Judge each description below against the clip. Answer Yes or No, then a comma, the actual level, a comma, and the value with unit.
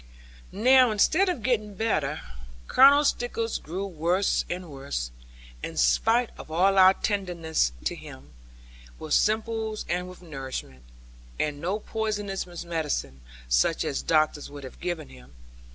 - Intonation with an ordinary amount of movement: No, wide, 6.9 semitones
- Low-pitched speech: No, medium, 180 Hz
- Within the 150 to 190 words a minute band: No, slow, 135 wpm